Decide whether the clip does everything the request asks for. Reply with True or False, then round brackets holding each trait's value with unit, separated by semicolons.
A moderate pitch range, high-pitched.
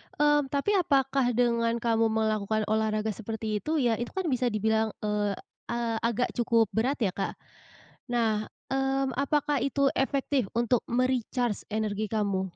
True (3.6 semitones; 235 Hz)